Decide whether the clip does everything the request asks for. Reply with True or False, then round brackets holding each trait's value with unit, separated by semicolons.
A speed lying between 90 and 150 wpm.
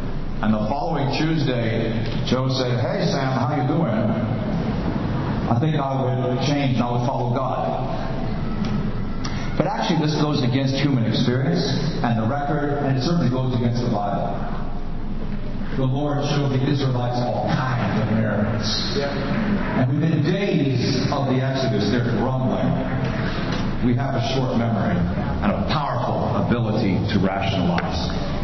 True (140 wpm)